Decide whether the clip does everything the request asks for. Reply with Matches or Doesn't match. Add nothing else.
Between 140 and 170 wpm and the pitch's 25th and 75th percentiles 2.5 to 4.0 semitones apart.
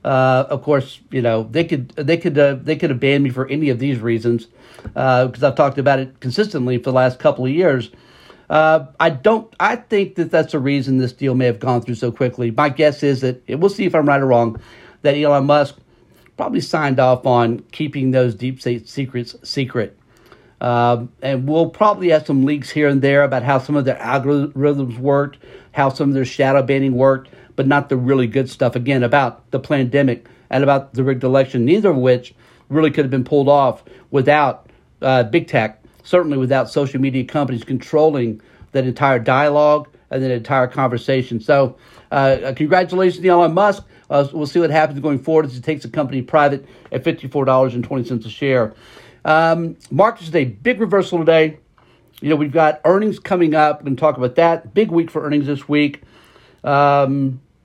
Doesn't match